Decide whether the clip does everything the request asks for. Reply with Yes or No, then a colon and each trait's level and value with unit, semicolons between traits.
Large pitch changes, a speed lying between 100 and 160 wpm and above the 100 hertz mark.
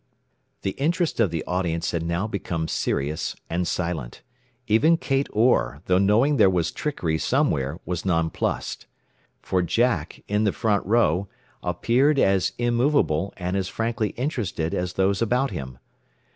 No: wide, 5.8 semitones; average, 145 wpm; very low, 95 Hz